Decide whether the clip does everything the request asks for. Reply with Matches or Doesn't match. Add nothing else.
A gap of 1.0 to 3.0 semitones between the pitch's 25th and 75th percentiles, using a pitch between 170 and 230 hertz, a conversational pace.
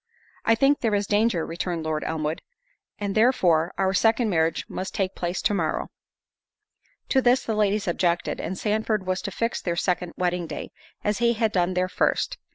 Doesn't match